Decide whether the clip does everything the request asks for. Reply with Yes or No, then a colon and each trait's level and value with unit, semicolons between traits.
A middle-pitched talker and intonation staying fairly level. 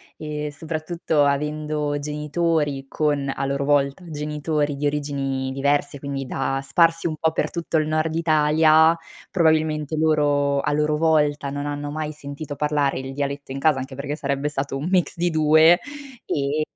Yes: medium, 150 Hz; narrow, 1.8 semitones